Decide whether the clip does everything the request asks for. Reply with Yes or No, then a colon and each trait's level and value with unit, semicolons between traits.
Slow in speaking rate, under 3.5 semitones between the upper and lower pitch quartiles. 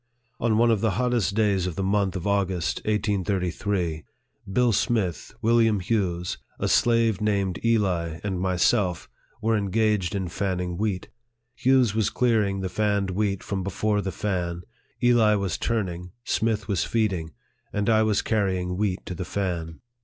No: average, 155 wpm; average, 3.1 semitones